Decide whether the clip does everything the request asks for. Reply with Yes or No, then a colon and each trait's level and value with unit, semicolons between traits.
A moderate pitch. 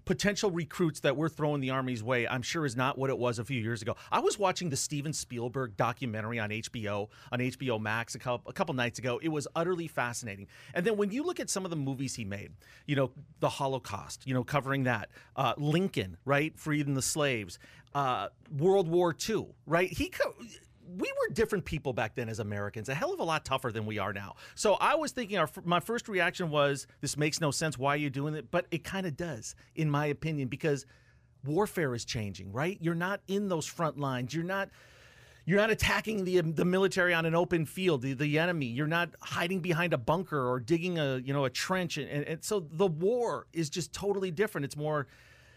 Yes: medium, 150 Hz